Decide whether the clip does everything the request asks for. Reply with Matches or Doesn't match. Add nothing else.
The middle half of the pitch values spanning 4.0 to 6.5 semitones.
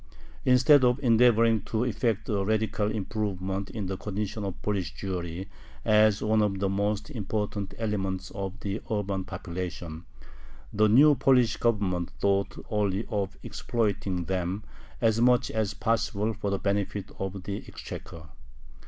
Doesn't match